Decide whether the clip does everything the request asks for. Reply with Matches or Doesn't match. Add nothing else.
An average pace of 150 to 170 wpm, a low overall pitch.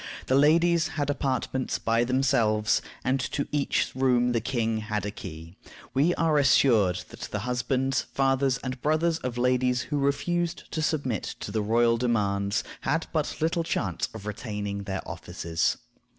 Matches